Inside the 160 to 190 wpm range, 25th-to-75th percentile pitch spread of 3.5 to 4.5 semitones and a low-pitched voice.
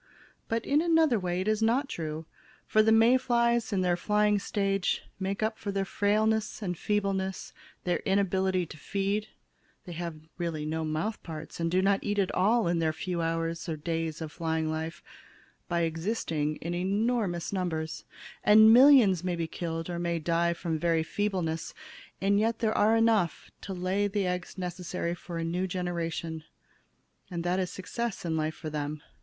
No: average, 180 wpm; average, 4.0 semitones; medium, 180 Hz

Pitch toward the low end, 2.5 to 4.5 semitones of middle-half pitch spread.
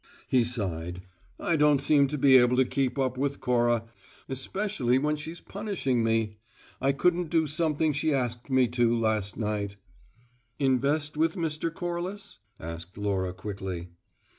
No: low, 130 Hz; average, 5.2 semitones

